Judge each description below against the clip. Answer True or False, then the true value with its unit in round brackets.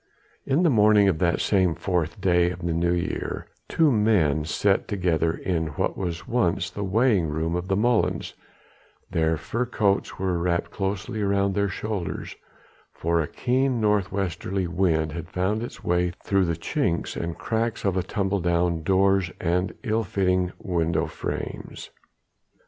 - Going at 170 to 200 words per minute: False (155 wpm)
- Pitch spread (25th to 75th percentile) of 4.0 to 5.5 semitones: False (3.2 semitones)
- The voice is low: True (95 Hz)